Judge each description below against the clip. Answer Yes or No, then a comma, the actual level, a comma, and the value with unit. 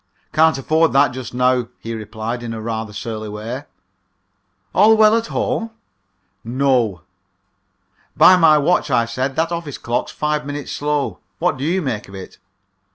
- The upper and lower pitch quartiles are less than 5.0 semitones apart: No, wide, 5.5 semitones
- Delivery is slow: No, average, 155 wpm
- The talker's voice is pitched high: No, low, 135 Hz